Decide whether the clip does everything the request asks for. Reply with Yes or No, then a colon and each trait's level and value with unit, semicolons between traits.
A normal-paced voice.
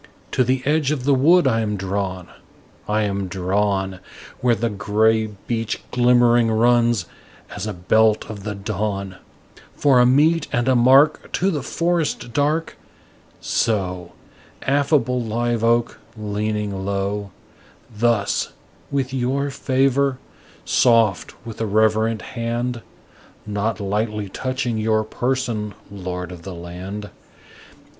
No: slow, 125 wpm